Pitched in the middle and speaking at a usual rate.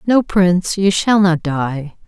Yes: medium, 180 Hz; average, 175 wpm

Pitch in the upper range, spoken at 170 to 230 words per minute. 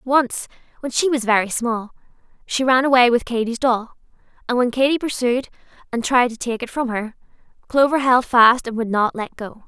Yes: high, 245 Hz; average, 190 wpm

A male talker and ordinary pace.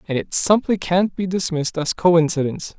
Yes: male; average, 170 wpm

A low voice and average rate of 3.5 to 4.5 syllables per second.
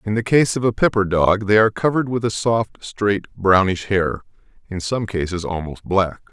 Yes: low, 100 Hz; 4.3 syllables/s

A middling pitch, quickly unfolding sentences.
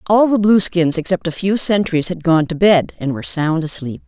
Yes: medium, 175 Hz; fast, 220 wpm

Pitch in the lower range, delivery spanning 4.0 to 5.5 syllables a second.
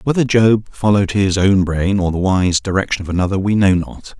Yes: very low, 95 Hz; 5.4 syllables/s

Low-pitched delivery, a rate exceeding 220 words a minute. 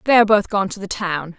No: high, 195 Hz; fast, 260 wpm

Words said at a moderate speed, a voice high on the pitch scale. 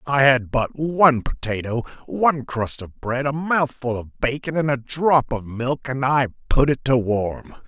No: average, 190 wpm; low, 130 Hz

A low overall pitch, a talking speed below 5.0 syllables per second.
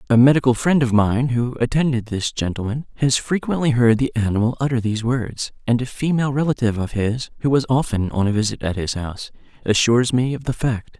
No: low, 120 Hz; 5.9 syllables/s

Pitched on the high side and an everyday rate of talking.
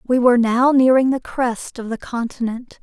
Yes: high, 245 Hz; average, 190 wpm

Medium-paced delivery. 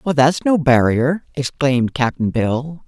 Yes: average, 145 wpm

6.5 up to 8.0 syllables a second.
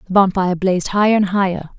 Yes: 7.1 syllables/s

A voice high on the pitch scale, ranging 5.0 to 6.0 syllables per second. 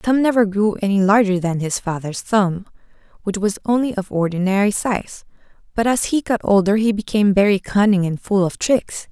Yes: high, 205 Hz; 5.2 syllables/s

